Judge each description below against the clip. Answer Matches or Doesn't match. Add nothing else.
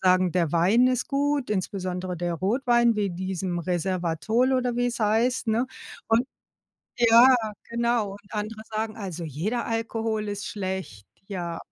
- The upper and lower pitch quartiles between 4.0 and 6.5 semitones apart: Matches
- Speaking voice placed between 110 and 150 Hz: Doesn't match